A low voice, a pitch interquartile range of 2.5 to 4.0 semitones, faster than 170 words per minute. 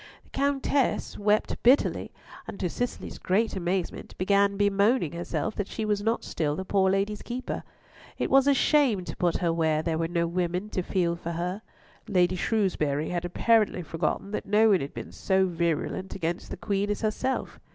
No: high, 190 Hz; average, 3.7 semitones; average, 185 wpm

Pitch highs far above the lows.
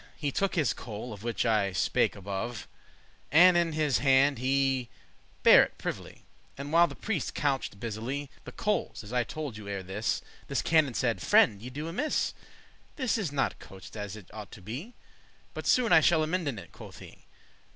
Yes: wide, 6.7 semitones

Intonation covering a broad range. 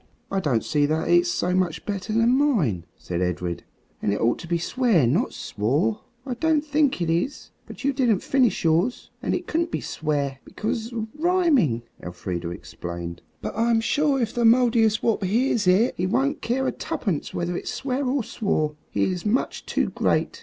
Yes: wide, 8.7 semitones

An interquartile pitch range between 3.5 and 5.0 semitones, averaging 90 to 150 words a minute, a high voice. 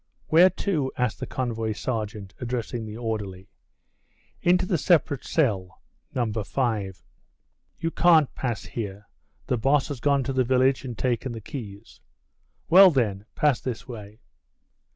No: average, 4.4 semitones; average, 140 wpm; low, 120 Hz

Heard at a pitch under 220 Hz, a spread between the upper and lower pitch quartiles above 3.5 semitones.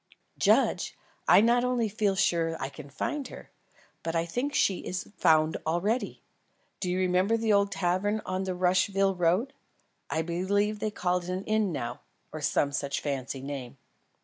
Yes: medium, 185 Hz; average, 4.1 semitones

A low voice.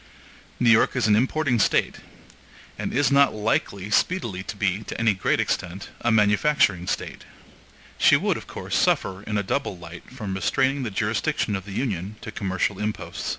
Yes: low, 105 Hz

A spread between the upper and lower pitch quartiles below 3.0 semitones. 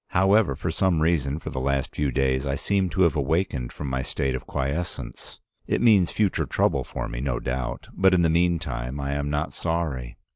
No: average, 4.7 semitones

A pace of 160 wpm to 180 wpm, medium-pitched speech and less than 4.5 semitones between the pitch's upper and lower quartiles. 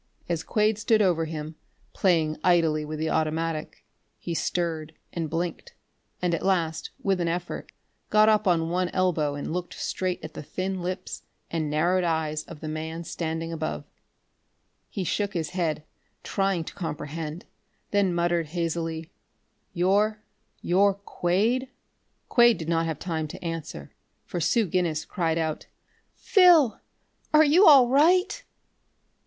No: average, 145 wpm; medium, 170 Hz; average, 3.2 semitones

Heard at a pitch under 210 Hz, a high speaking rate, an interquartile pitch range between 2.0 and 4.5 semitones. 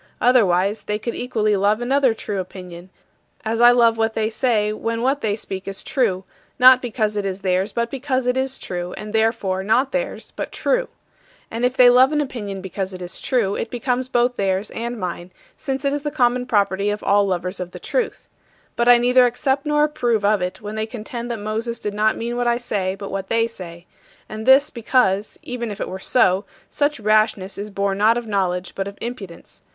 No: high, 220 Hz; fast, 210 wpm; average, 3.9 semitones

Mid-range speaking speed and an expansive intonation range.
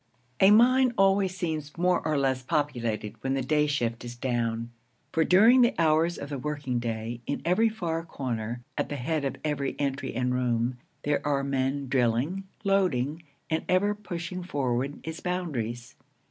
Yes: average, 165 wpm; wide, 5.9 semitones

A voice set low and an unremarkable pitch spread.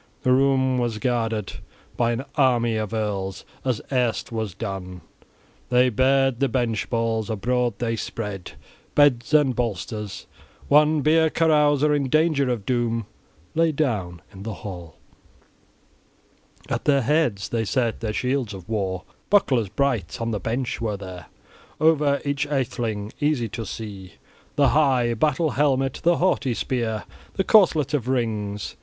Yes: low, 120 Hz; average, 4.5 semitones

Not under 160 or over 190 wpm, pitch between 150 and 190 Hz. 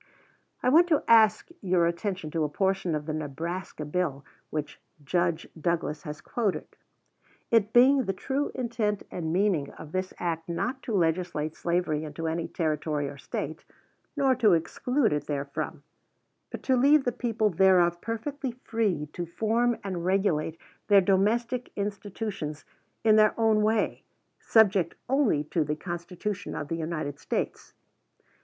No: average, 150 wpm; medium, 185 Hz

